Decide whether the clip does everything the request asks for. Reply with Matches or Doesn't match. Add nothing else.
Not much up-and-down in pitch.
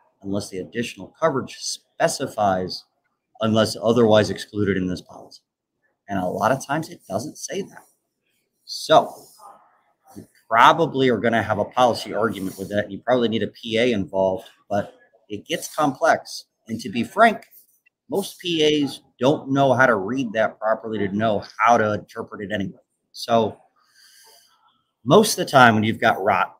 Doesn't match